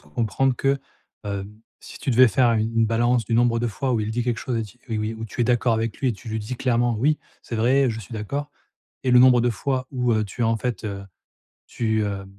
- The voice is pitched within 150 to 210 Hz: No, low, 115 Hz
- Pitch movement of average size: No, narrow, 2.2 semitones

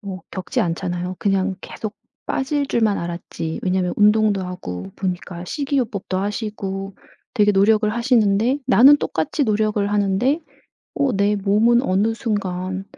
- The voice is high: Yes, high, 205 Hz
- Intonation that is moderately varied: Yes, average, 3.1 semitones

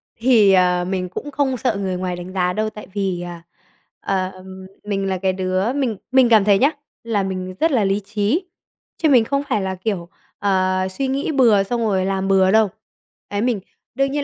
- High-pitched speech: Yes, high, 200 Hz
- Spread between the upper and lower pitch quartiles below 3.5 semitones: No, average, 4.1 semitones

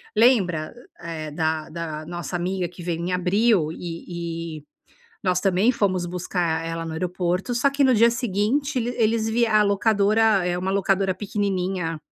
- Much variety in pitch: No, average, 4.0 semitones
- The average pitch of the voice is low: No, medium, 185 Hz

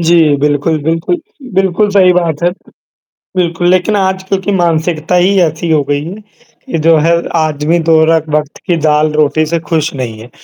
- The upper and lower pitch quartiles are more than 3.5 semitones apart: No, narrow, 2.6 semitones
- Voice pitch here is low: No, medium, 165 Hz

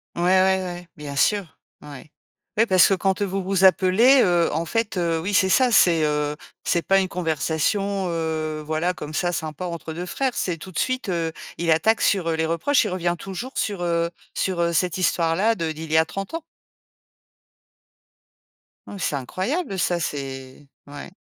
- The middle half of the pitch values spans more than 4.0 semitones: No, average, 3.3 semitones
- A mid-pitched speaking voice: Yes, medium, 175 Hz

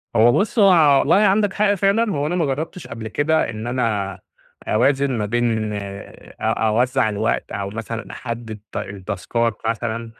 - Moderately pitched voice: No, low, 120 Hz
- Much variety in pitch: Yes, wide, 6.4 semitones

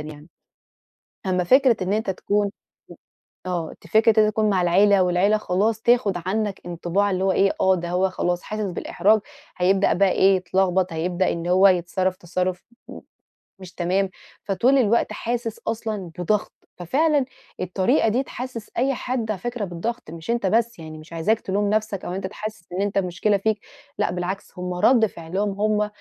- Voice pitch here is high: Yes, high, 195 Hz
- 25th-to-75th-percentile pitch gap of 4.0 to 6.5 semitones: No, average, 3.2 semitones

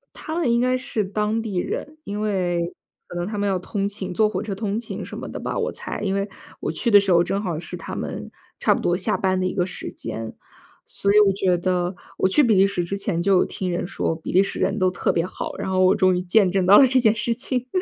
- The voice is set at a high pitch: Yes, high, 195 Hz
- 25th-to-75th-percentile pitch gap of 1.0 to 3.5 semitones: Yes, average, 2.8 semitones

